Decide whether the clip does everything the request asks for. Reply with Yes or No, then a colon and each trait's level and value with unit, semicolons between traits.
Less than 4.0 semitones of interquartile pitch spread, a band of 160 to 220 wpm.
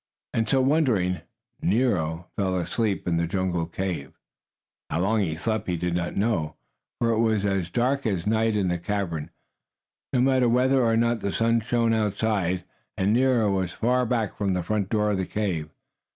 No: average, 4.4 semitones; average, 180 wpm